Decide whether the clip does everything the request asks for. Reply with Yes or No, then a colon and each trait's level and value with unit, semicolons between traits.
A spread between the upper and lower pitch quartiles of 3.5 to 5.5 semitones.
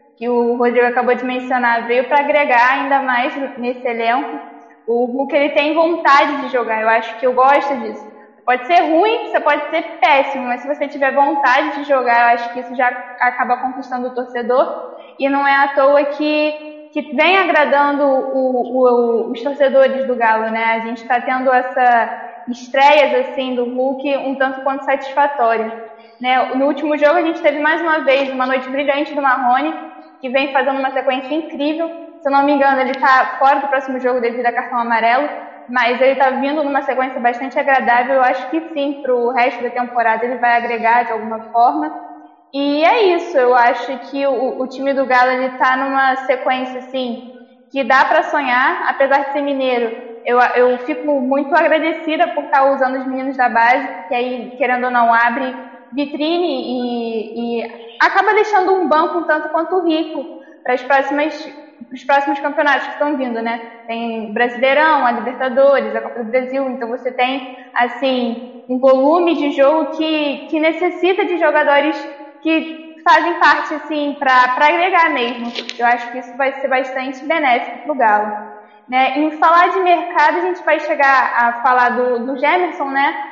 No: average, 3.0 semitones